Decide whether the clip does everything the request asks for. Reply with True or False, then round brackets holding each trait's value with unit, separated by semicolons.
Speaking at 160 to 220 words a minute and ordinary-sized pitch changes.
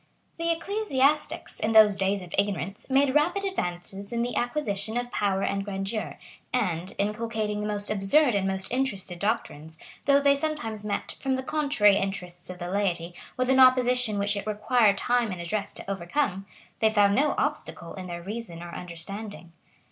True (175 wpm; 4.7 semitones)